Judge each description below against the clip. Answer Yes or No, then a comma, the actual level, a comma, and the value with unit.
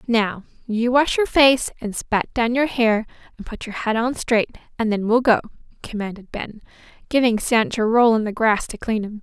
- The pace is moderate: No, fast, 210 wpm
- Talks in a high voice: Yes, high, 230 Hz